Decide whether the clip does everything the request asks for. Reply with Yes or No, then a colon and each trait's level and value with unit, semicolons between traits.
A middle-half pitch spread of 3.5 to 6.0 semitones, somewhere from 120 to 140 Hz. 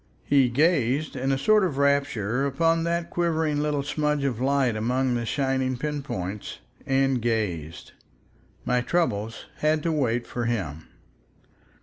Yes: average, 4.0 semitones; low, 135 Hz